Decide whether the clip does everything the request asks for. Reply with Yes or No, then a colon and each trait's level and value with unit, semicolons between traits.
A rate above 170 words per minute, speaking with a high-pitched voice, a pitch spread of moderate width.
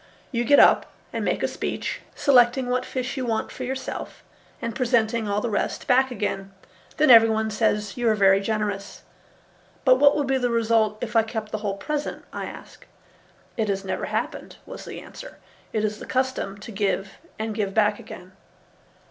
Yes: average, 185 wpm; high, 225 Hz; average, 3.3 semitones